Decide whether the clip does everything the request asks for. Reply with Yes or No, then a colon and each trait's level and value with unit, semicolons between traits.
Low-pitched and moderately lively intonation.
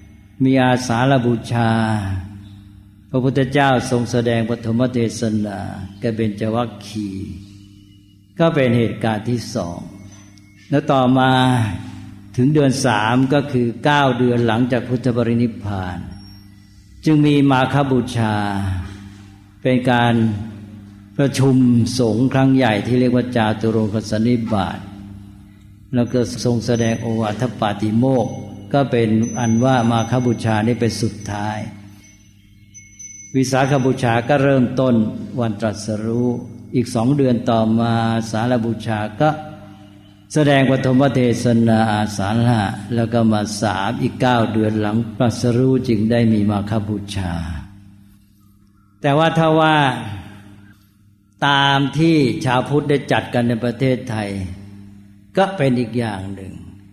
Yes: low, 115 Hz; average, 3.8 semitones